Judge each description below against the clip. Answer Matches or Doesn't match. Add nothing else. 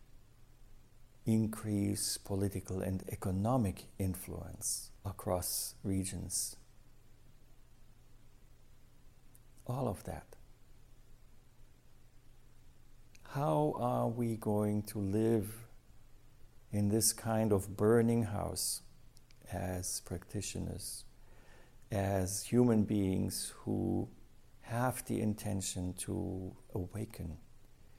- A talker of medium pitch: Doesn't match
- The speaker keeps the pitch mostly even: Doesn't match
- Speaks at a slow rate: Matches